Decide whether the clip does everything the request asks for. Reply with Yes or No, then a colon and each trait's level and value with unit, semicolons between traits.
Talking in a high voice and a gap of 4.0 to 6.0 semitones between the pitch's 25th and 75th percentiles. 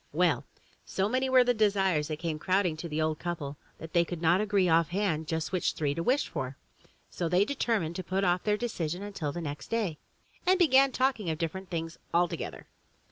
No: medium, 175 Hz; average, 4.4 semitones